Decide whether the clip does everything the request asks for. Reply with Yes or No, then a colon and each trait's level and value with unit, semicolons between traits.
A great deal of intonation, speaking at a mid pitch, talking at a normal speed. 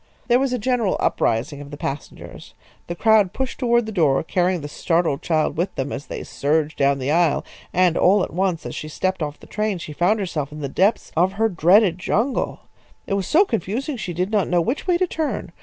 No: wide, 6.0 semitones; medium, 180 Hz; fast, 225 wpm